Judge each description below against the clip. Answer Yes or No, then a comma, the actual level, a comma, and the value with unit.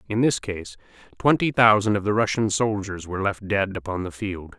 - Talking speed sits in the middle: Yes, average, 195 wpm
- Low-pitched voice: Yes, low, 100 Hz